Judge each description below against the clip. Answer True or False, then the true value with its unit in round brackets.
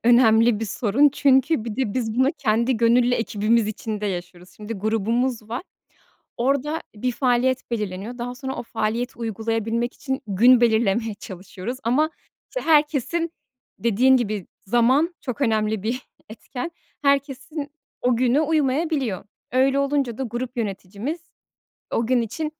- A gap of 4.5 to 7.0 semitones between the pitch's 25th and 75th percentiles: False (3.3 semitones)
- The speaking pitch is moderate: False (240 Hz)